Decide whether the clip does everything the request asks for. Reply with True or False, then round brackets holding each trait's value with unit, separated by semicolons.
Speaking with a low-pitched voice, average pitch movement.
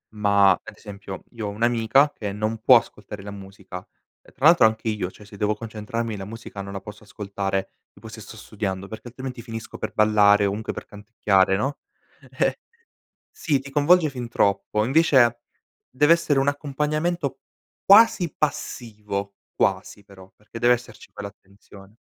True (110 Hz; 4.1 semitones)